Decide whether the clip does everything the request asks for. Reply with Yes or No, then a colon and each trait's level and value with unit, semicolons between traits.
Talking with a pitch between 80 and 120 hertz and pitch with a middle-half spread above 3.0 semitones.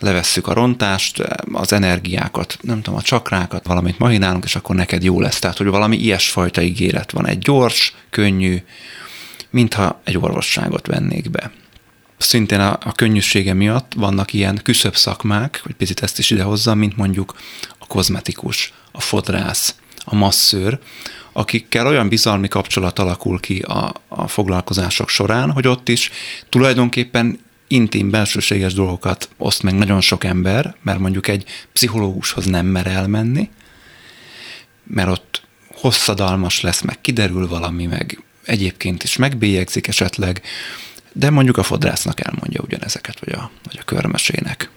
Yes: low, 100 Hz; average, 3.5 semitones